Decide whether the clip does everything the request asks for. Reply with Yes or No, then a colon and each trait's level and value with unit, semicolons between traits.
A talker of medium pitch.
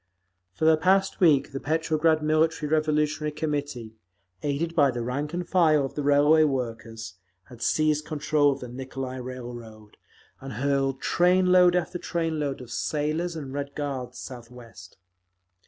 Yes: medium, 145 Hz